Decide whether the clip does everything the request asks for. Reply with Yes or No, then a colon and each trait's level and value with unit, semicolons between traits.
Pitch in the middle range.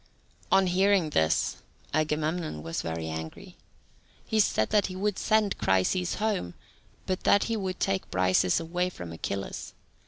Yes: medium, 175 Hz